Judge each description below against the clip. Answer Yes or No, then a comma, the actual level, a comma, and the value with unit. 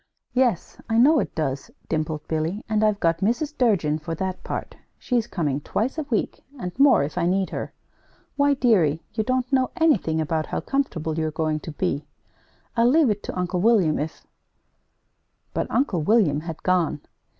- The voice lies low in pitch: No, medium, 185 Hz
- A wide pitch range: Yes, wide, 7.3 semitones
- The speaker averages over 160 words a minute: Yes, average, 180 wpm